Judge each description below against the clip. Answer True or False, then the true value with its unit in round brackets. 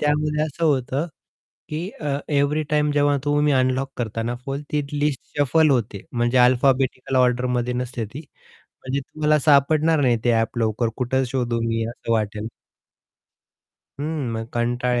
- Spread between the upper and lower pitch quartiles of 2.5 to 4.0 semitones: True (3.5 semitones)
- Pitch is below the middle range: True (130 Hz)